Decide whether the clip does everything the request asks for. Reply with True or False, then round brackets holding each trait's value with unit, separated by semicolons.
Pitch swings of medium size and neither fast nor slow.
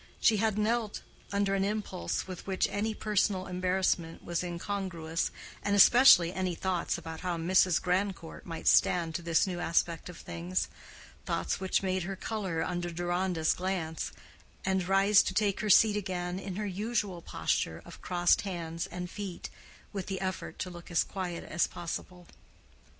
False (2.3 semitones; 160 wpm)